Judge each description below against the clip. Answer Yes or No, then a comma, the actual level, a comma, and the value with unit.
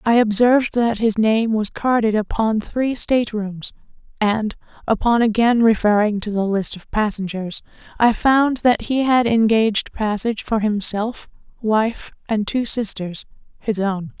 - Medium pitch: No, high, 220 Hz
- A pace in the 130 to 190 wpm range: Yes, average, 145 wpm